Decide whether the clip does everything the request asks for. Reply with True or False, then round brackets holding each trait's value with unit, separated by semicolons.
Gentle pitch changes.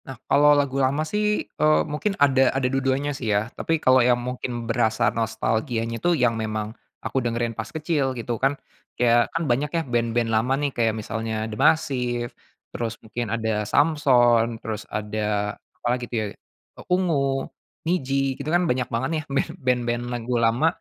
False (3.3 semitones)